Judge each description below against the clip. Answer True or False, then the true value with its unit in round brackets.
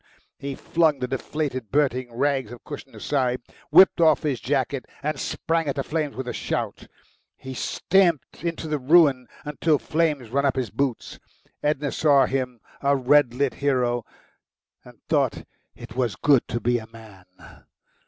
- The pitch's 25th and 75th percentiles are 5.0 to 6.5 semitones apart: False (3.1 semitones)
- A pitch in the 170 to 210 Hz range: False (135 Hz)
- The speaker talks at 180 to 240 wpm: False (160 wpm)